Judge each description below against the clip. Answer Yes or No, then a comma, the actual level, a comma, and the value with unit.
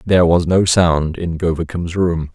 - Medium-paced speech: Yes, average, 180 wpm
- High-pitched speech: No, very low, 85 Hz